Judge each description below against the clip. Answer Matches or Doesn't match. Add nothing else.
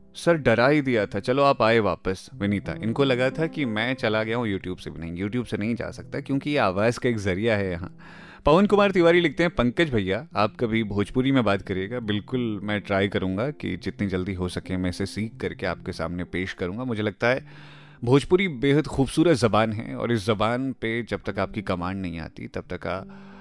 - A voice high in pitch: Doesn't match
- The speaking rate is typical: Doesn't match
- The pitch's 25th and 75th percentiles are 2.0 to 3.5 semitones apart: Doesn't match